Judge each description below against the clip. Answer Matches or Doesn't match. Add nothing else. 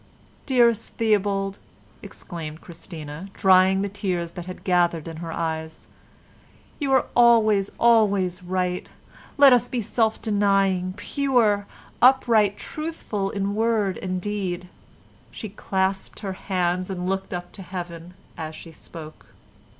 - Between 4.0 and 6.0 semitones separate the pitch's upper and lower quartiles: Doesn't match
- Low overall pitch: Doesn't match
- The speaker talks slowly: Matches